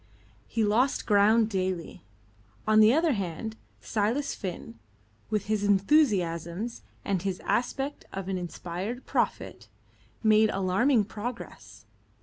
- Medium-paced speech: No, slow, 115 wpm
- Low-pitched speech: No, high, 210 Hz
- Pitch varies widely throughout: No, average, 3.6 semitones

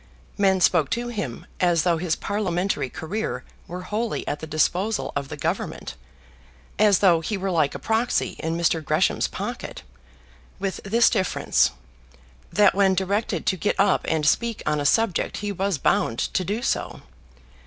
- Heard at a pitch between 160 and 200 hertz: Yes, high, 190 Hz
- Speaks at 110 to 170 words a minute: Yes, average, 165 wpm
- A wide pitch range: No, average, 4.2 semitones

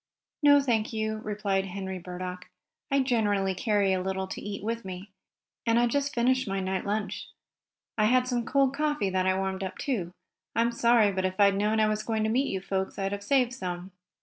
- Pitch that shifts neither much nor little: Yes, average, 3.8 semitones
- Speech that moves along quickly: Yes, fast, 210 wpm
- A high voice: Yes, high, 210 Hz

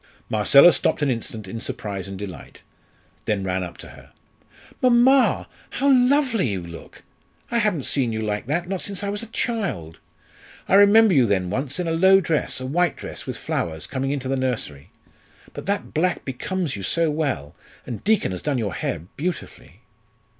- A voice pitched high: No, medium, 140 Hz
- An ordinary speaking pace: Yes, average, 180 wpm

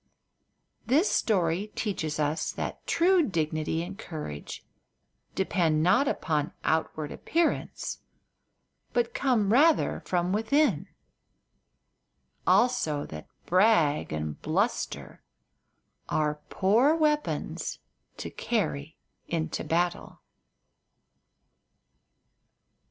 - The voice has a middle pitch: Yes, medium, 180 Hz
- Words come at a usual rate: No, slow, 80 wpm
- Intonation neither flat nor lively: No, wide, 7.6 semitones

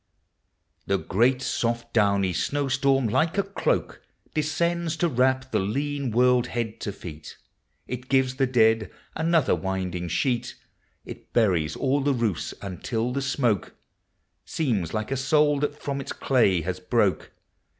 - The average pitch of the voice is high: No, low, 125 Hz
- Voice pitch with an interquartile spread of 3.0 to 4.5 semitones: No, average, 5.1 semitones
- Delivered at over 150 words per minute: No, average, 145 wpm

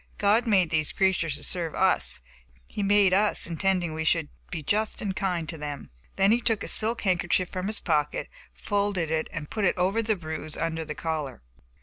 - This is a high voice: No, medium, 180 Hz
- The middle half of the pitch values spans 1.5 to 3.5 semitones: No, average, 4.2 semitones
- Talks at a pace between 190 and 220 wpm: Yes, average, 200 wpm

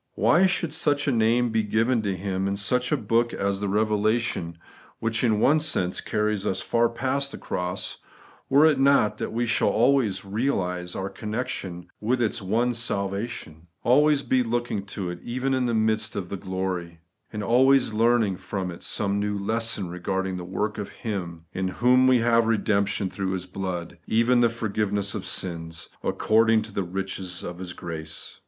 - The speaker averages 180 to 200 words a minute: Yes, average, 185 wpm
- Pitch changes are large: No, average, 3.9 semitones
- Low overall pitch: Yes, low, 105 Hz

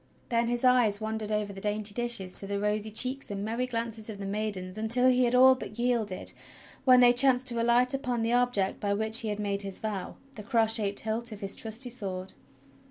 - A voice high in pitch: Yes, high, 220 Hz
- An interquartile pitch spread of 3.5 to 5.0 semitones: No, average, 3.1 semitones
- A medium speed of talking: No, fast, 230 wpm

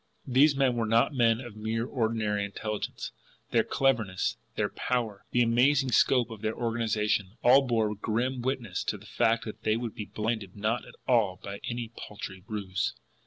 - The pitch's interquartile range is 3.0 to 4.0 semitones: No, narrow, 2.4 semitones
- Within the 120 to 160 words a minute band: No, average, 170 wpm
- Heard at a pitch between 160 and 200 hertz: No, low, 115 Hz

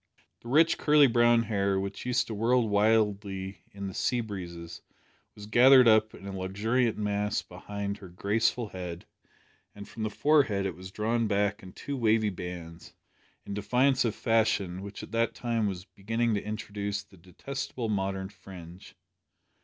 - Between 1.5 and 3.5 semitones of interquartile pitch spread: Yes, average, 3.0 semitones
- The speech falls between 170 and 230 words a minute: No, average, 160 wpm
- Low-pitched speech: Yes, low, 105 Hz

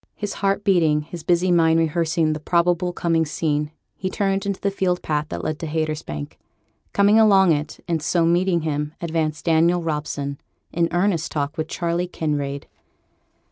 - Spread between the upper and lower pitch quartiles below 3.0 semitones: Yes, narrow, 2.6 semitones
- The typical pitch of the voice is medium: Yes, medium, 165 Hz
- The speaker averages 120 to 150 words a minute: No, average, 165 wpm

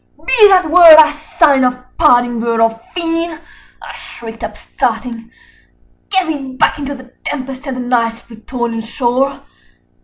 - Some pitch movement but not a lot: Yes, average, 4.7 semitones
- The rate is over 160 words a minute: No, average, 145 wpm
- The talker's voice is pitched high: Yes, very high, 260 Hz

